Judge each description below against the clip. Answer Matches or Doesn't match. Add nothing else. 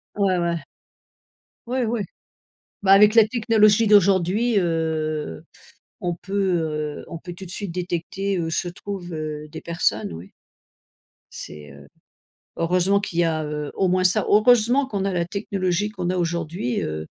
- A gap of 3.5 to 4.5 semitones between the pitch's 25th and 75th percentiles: Matches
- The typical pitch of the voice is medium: Matches